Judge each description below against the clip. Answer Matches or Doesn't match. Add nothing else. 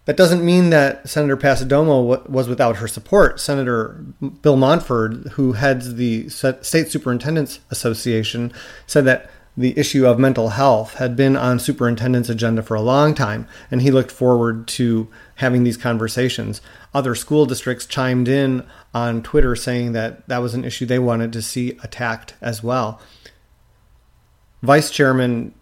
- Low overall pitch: Matches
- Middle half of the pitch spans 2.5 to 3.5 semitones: Matches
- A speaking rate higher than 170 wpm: Doesn't match